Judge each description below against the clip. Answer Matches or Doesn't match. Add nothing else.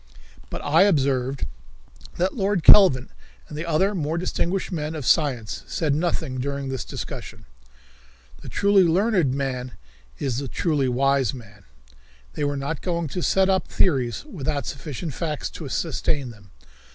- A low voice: Doesn't match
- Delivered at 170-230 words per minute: Doesn't match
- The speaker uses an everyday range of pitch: Matches